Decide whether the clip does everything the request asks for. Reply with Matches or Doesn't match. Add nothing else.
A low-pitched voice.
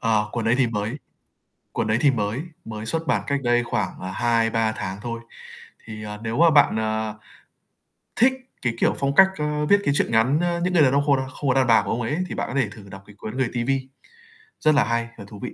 Matches